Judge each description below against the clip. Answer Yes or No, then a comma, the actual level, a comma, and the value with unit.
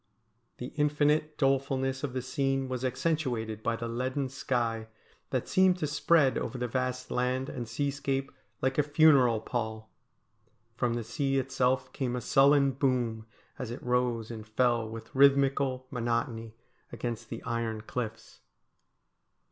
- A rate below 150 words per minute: Yes, average, 140 wpm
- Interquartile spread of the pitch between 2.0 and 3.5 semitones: Yes, narrow, 2.6 semitones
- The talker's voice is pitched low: Yes, low, 130 Hz